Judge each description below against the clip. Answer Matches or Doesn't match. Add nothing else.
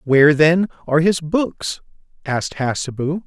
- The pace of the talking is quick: Doesn't match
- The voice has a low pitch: Doesn't match